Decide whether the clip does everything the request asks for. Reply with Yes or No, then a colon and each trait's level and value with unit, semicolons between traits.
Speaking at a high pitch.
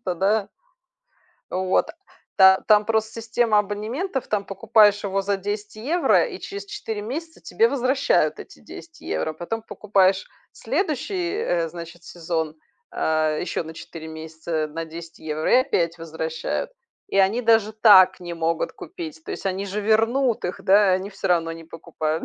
Yes: high, 200 Hz